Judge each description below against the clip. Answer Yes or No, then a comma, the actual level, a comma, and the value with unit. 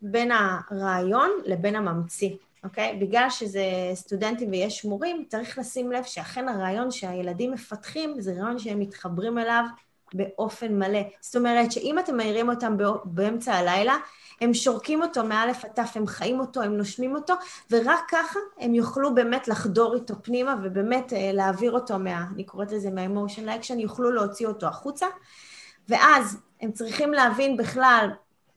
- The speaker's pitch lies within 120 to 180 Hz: No, high, 225 Hz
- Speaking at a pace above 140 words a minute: Yes, fast, 150 wpm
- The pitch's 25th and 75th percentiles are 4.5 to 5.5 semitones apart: No, average, 3.8 semitones